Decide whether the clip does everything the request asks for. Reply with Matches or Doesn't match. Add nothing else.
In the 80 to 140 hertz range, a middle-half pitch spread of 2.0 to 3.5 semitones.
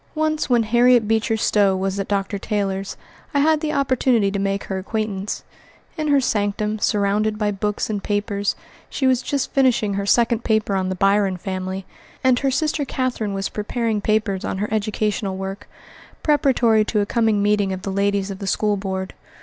Doesn't match